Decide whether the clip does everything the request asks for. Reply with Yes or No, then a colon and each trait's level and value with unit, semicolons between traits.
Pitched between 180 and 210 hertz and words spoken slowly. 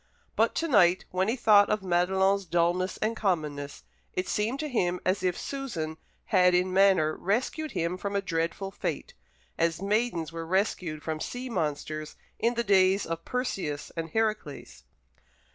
No: medium, 185 Hz; average, 160 wpm